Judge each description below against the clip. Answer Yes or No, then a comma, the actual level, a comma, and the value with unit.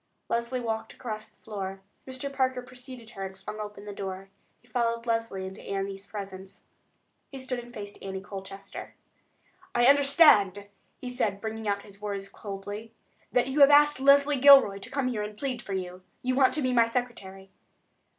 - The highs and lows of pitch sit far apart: No, average, 4.4 semitones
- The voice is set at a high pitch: Yes, high, 220 Hz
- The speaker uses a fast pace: No, average, 180 wpm